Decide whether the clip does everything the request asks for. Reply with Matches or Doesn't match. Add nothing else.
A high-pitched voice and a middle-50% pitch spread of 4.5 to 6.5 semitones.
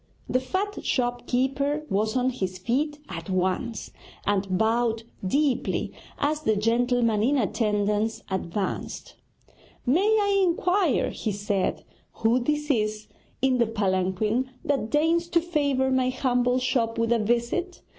Matches